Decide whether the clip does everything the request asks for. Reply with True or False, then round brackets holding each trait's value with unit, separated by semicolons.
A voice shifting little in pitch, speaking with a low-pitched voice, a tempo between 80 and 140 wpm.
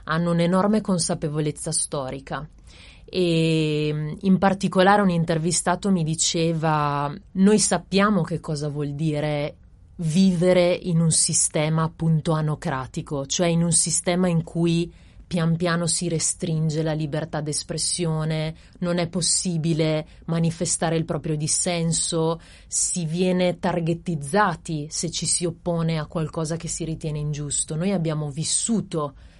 False (2.1 semitones; 165 Hz; 120 wpm)